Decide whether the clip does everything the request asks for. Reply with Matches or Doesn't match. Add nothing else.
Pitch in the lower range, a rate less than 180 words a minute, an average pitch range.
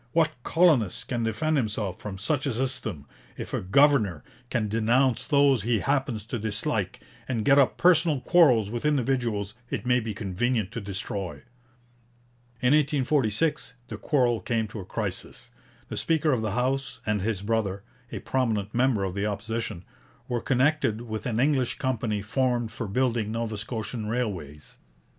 Matches